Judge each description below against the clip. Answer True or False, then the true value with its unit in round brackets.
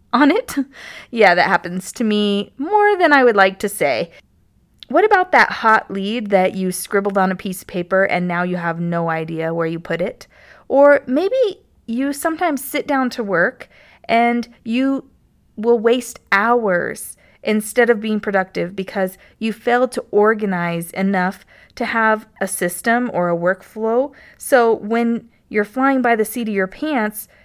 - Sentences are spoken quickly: False (170 wpm)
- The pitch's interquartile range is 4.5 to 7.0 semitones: True (4.8 semitones)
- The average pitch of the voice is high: True (220 Hz)